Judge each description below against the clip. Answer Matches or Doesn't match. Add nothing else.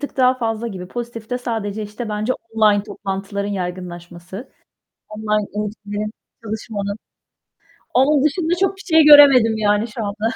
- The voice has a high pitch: Matches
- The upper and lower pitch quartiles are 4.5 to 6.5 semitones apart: Doesn't match